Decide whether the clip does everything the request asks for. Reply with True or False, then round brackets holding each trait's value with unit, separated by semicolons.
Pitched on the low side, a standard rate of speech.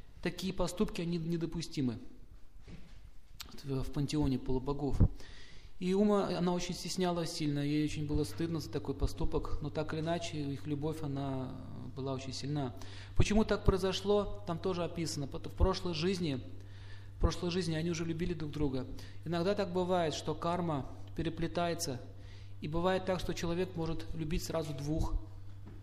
False (155 Hz; 145 wpm)